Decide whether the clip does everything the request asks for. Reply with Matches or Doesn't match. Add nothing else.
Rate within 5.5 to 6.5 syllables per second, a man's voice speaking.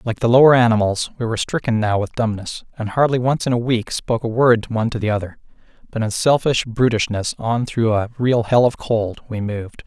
Matches